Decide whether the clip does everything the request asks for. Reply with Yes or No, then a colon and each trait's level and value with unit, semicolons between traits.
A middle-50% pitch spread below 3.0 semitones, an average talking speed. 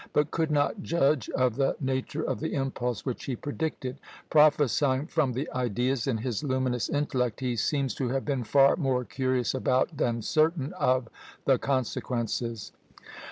Yes: narrow, 2.6 semitones; average, 160 wpm